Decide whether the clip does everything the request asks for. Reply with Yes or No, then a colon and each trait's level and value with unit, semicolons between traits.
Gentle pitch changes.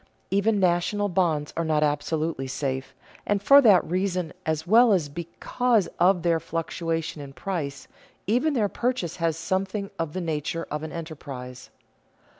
No: average, 4.3 semitones